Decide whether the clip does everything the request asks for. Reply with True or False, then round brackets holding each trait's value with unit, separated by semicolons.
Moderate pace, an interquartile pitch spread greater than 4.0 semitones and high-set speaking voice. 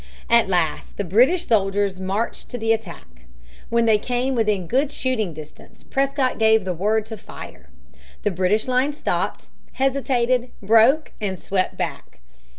True (150 wpm; 4.5 semitones; 220 Hz)